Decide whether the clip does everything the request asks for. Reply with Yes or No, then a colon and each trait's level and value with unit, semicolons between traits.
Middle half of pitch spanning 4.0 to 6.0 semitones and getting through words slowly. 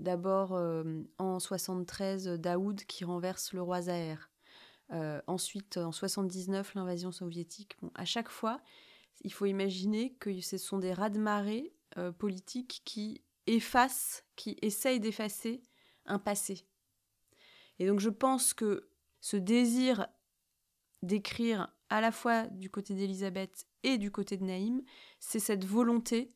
No: average, 3.6 semitones; slow, 140 wpm